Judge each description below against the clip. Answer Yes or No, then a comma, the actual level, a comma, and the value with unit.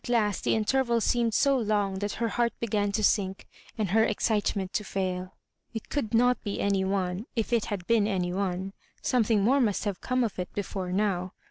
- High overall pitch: Yes, high, 210 Hz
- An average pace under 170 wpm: No, fast, 205 wpm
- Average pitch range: Yes, average, 3.2 semitones